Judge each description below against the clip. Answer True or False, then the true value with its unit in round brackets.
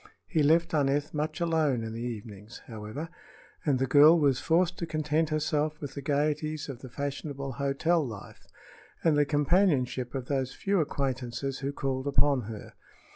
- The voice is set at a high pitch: False (140 Hz)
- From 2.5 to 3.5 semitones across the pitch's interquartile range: True (2.9 semitones)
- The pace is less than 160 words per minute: False (165 wpm)